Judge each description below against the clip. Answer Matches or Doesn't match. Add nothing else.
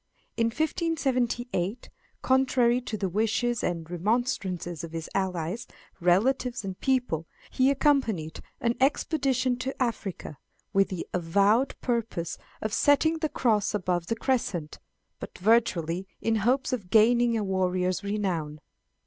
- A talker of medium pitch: Doesn't match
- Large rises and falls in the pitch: Matches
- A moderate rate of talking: Doesn't match